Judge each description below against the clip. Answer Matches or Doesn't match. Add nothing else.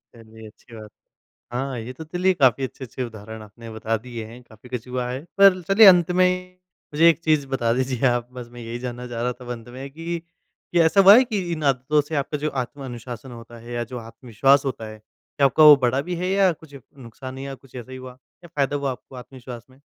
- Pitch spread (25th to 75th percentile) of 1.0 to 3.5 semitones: Doesn't match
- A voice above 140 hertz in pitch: Doesn't match